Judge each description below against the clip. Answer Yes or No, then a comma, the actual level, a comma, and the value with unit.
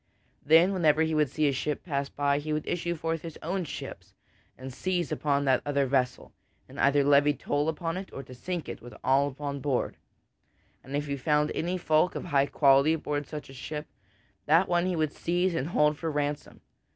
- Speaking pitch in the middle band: Yes, medium, 150 Hz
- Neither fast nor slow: No, fast, 210 wpm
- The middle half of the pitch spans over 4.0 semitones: No, narrow, 2.6 semitones